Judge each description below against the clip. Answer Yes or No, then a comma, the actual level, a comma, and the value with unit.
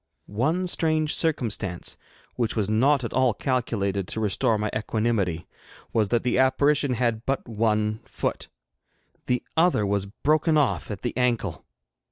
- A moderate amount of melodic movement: Yes, average, 4.2 semitones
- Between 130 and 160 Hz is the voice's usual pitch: No, low, 115 Hz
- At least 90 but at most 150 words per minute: Yes, average, 145 wpm